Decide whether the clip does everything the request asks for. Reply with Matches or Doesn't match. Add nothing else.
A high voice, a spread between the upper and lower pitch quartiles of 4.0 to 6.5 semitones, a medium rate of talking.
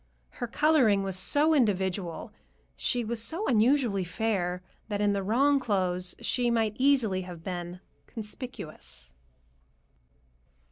Doesn't match